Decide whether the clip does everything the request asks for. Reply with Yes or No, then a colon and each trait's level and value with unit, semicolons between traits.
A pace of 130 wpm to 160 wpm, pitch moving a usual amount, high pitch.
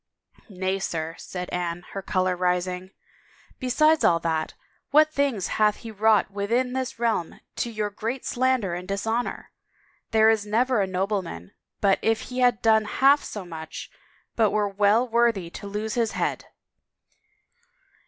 Yes: average, 155 wpm; average, 4.2 semitones; high, 210 Hz